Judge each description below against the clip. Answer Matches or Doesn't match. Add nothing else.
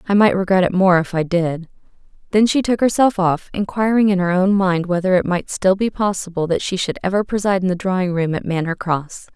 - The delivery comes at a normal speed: Doesn't match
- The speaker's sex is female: Matches